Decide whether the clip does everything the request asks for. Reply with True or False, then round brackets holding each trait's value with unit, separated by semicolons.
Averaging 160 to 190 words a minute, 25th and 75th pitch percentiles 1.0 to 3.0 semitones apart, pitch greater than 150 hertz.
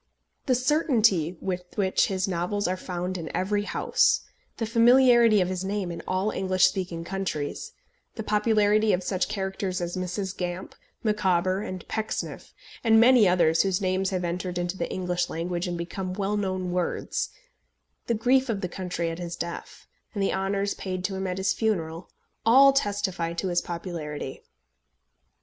True (165 wpm; 2.7 semitones; 190 Hz)